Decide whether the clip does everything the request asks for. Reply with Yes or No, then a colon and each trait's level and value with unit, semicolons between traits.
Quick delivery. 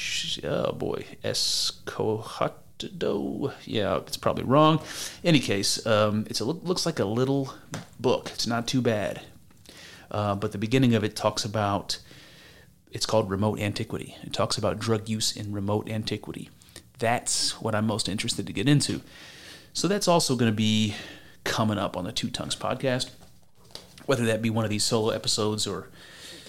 No: average, 160 wpm